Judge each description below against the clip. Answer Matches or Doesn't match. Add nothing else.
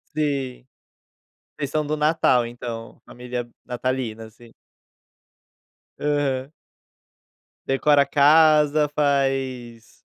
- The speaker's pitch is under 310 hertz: Matches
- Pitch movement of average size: Matches